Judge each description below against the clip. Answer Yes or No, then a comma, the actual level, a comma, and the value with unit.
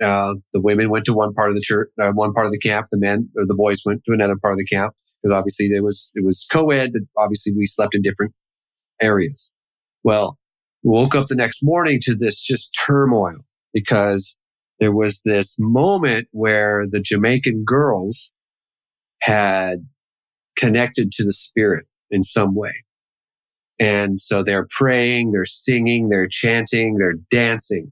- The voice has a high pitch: No, low, 105 Hz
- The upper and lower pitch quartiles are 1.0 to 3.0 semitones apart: Yes, narrow, 2.6 semitones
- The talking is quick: No, average, 170 wpm